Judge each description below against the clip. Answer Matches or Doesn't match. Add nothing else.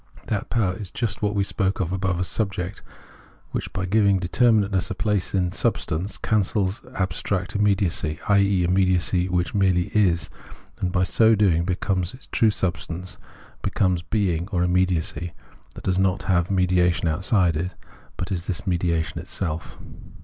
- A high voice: Doesn't match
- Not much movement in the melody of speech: Matches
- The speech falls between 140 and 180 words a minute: Matches